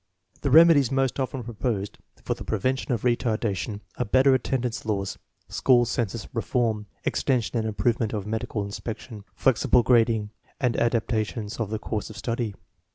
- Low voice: Yes, low, 115 Hz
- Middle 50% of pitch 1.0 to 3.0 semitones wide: Yes, narrow, 2.6 semitones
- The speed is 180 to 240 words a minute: No, average, 150 wpm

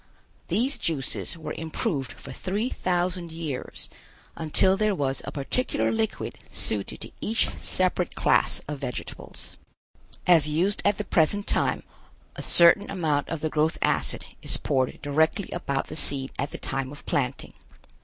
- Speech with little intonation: No, average, 4.7 semitones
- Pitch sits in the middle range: Yes, medium, 160 Hz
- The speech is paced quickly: No, average, 150 wpm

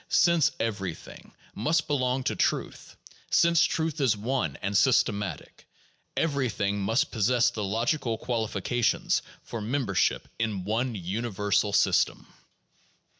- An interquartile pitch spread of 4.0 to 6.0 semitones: Yes, average, 4.4 semitones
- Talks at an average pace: No, slow, 115 wpm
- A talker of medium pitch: No, low, 115 Hz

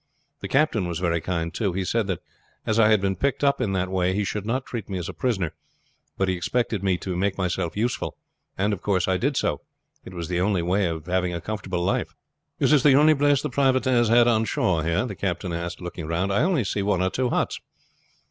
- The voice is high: No, very low, 95 Hz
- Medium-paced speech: No, fast, 240 wpm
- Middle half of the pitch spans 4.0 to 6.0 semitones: Yes, average, 4.9 semitones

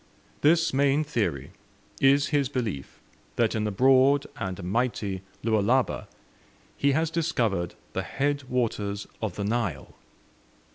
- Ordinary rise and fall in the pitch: No, wide, 5.7 semitones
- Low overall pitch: Yes, low, 120 Hz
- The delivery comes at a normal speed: No, slow, 125 wpm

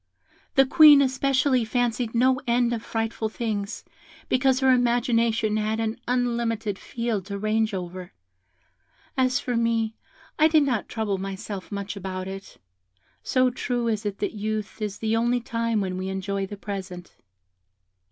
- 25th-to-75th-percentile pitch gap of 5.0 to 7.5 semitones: No, average, 3.3 semitones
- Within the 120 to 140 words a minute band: No, average, 150 wpm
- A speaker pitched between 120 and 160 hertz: No, high, 225 Hz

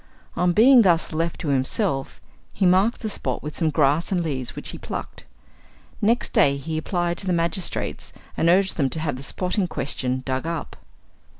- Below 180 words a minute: No, average, 190 wpm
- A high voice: No, medium, 165 Hz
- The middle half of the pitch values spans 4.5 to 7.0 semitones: Yes, average, 4.9 semitones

